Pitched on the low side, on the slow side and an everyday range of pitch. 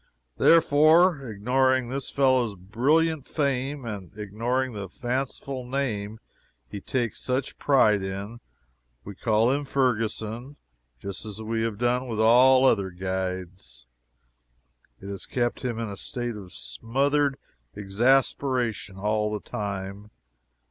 Yes: low, 115 Hz; slow, 120 wpm; average, 4.5 semitones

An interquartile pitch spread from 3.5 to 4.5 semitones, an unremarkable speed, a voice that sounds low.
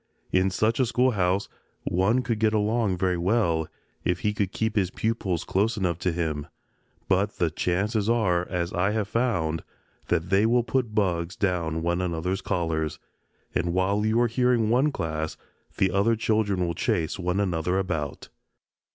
Yes: average, 4.1 semitones; average, 165 wpm; very low, 95 Hz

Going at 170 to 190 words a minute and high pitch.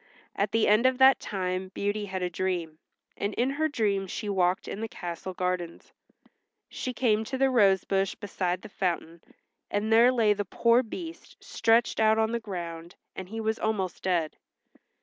Yes: average, 180 wpm; high, 205 Hz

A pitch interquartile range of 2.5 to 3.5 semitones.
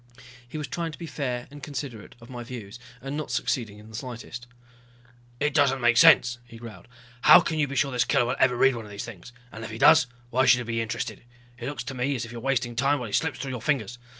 Yes: average, 2.9 semitones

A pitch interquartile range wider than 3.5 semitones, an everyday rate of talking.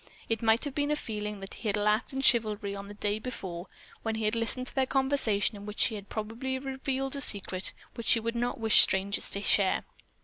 No: average, 4.0 semitones; fast, 230 wpm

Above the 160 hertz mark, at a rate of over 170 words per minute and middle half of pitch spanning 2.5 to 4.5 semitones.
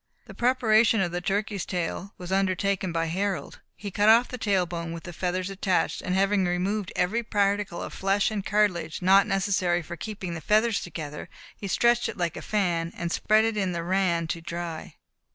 Yes: high, 190 Hz; average, 195 wpm; average, 3.0 semitones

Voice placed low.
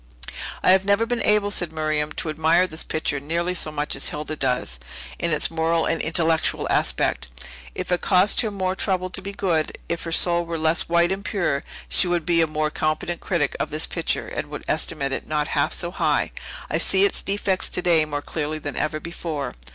No: medium, 165 Hz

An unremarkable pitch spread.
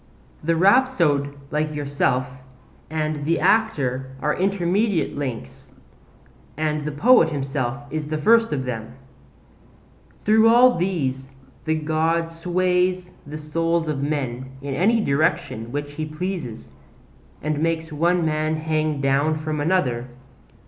Yes: average, 3.4 semitones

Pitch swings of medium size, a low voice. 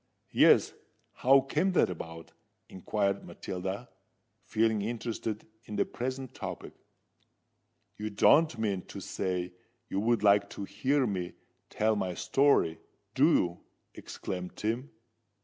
Yes: average, 4.5 semitones; low, 105 Hz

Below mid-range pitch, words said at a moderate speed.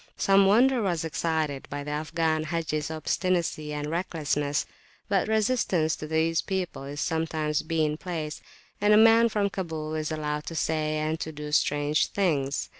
No: medium, 160 Hz; average, 160 wpm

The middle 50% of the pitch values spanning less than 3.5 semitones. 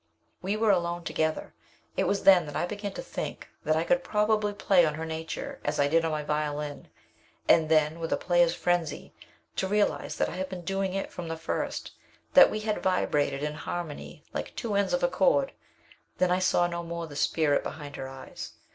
No: average, 4.0 semitones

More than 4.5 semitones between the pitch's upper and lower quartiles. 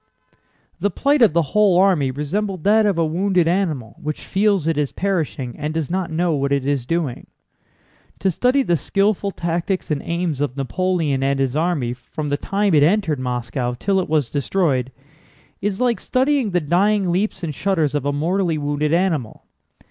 Yes: average, 5.3 semitones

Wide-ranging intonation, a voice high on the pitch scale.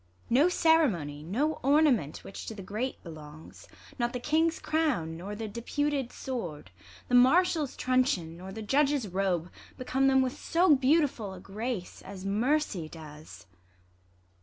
Yes: wide, 7.8 semitones; high, 240 Hz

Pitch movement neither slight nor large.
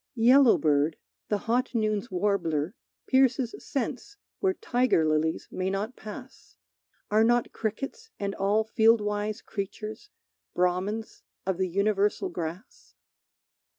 Yes: average, 4.2 semitones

